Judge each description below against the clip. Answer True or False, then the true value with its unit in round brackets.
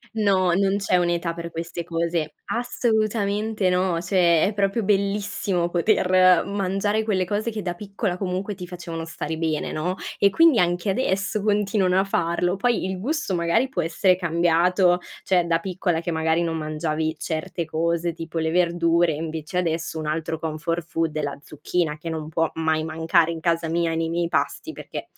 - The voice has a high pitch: False (175 Hz)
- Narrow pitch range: False (3.0 semitones)